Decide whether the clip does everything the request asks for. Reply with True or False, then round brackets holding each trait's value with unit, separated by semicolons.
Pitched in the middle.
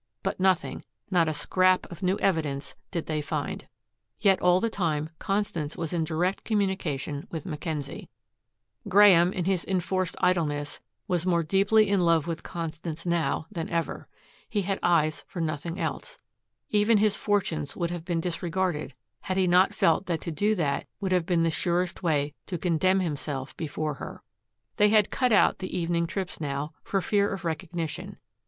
True (175 Hz)